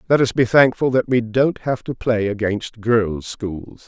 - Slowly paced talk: No, average, 200 wpm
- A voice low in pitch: Yes, low, 115 Hz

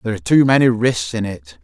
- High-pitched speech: No, low, 105 Hz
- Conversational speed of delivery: No, fast, 255 wpm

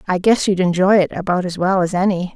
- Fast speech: Yes, fast, 255 wpm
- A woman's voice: Yes, female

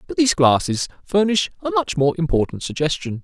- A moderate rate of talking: Yes, average, 165 wpm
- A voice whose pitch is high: No, medium, 180 Hz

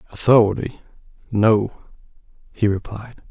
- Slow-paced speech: Yes, slow, 55 wpm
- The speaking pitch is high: No, low, 105 Hz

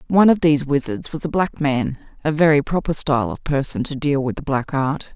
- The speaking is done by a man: No, female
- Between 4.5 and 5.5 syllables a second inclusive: No, 5.7 syllables/s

